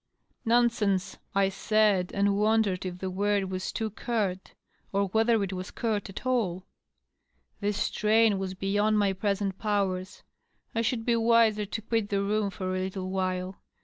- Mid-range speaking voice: No, high, 200 Hz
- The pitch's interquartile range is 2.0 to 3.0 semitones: Yes, narrow, 2.5 semitones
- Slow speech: No, average, 170 wpm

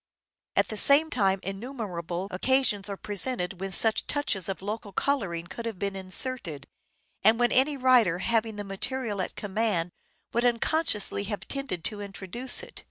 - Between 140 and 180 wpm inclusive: Yes, average, 160 wpm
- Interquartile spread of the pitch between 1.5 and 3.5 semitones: No, average, 4.6 semitones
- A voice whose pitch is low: No, high, 210 Hz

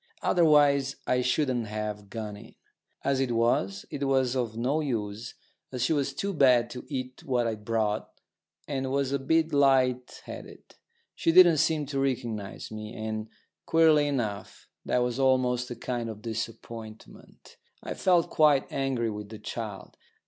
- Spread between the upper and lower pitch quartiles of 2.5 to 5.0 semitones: Yes, average, 3.9 semitones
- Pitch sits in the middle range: No, low, 125 Hz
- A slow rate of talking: No, average, 155 wpm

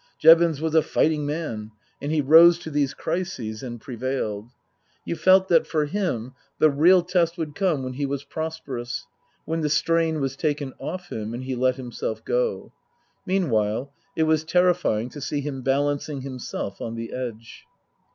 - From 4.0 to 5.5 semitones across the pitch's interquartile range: Yes, average, 4.3 semitones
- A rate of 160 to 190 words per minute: Yes, average, 170 wpm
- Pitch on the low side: No, medium, 145 Hz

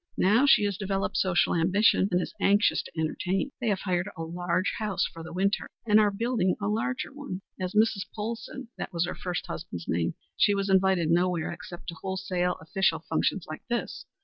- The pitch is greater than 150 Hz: Yes, high, 190 Hz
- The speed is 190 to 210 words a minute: Yes, average, 195 wpm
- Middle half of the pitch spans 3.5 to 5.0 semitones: No, average, 3.0 semitones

